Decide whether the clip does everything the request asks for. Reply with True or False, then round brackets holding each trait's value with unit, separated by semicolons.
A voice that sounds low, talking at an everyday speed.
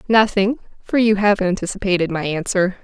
False (195 Hz; 150 wpm)